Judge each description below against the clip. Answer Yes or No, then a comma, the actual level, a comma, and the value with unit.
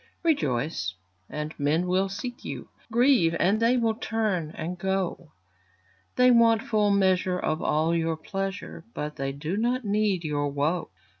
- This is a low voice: No, medium, 180 Hz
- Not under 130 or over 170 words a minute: Yes, average, 145 wpm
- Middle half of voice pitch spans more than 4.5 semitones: Yes, wide, 5.6 semitones